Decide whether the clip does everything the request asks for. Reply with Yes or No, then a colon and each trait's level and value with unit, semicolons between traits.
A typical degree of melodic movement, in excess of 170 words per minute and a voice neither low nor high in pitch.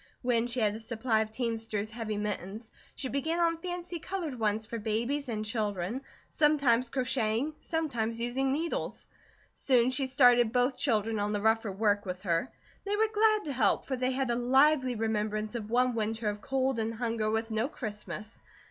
No: average, 3.5 semitones; average, 180 wpm; high, 235 Hz